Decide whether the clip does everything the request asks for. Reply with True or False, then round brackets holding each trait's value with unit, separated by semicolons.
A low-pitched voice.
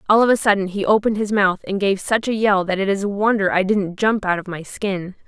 False (200 Hz)